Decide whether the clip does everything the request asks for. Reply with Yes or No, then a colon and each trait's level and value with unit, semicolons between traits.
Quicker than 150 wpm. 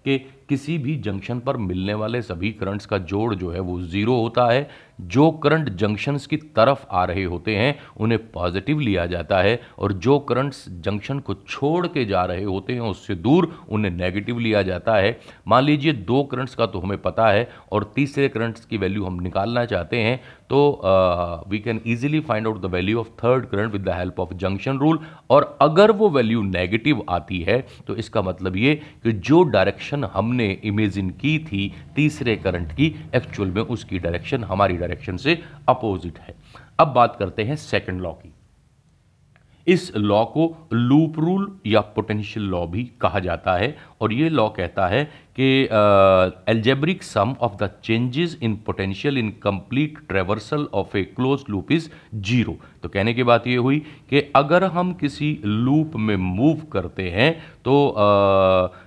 Yes: average, 175 wpm